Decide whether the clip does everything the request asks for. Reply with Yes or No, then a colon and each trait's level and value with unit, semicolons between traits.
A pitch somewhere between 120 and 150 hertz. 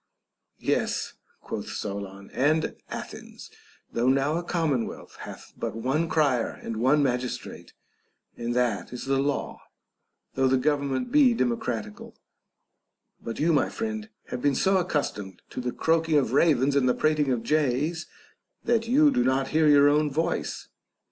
Yes: medium, 140 Hz